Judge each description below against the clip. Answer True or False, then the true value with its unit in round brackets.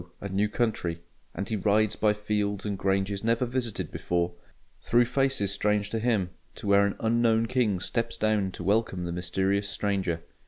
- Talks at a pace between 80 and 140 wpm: False (170 wpm)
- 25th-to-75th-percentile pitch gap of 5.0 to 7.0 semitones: False (2.6 semitones)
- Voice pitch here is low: True (105 Hz)